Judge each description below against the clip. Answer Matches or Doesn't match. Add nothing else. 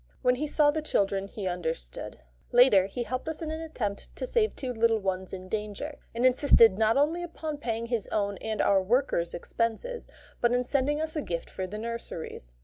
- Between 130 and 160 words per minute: Doesn't match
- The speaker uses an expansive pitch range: Matches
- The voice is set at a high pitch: Matches